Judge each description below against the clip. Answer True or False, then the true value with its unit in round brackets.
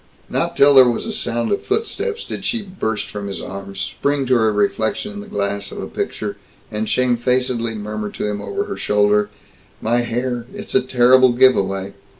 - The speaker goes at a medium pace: True (185 wpm)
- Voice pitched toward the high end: False (120 Hz)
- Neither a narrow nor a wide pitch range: True (3.9 semitones)